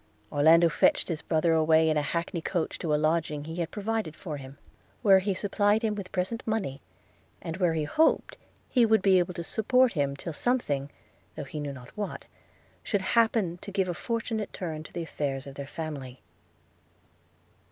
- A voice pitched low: No, medium, 170 Hz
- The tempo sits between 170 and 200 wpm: Yes, average, 185 wpm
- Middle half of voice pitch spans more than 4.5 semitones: Yes, average, 5.2 semitones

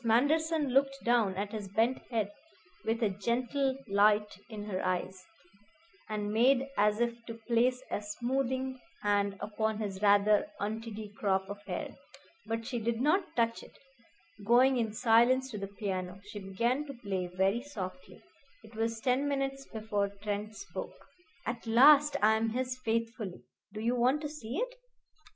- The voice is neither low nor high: No, high, 225 Hz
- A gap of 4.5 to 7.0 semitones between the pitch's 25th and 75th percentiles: No, average, 3.7 semitones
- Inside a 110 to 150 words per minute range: No, average, 160 wpm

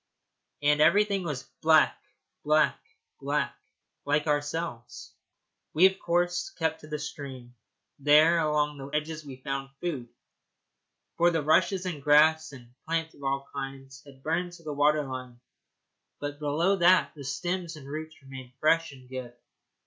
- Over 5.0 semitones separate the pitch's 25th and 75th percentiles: No, average, 3.2 semitones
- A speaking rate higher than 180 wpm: No, average, 150 wpm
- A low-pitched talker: No, medium, 150 Hz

